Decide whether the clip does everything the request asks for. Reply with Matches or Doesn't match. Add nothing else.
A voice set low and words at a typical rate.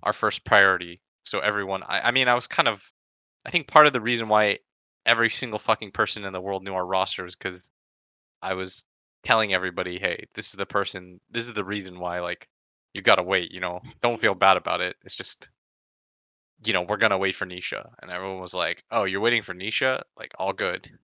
Doesn't match